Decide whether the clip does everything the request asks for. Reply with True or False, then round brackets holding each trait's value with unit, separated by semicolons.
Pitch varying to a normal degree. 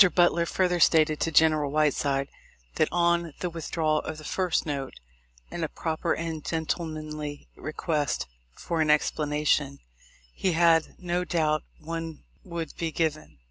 False (1.8 semitones)